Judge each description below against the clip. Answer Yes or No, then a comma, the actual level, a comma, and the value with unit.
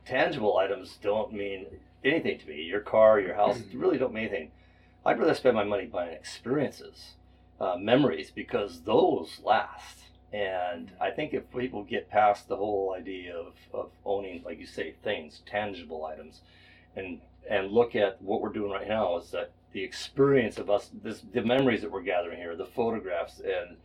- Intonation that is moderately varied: Yes, average, 3.5 semitones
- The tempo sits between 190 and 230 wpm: No, average, 180 wpm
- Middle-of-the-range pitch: No, low, 105 Hz